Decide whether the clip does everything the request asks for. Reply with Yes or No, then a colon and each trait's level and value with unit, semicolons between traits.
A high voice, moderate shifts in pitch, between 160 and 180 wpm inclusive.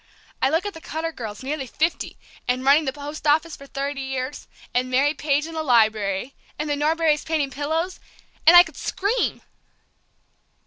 Yes: very high, 290 Hz; average, 3.2 semitones; average, 175 wpm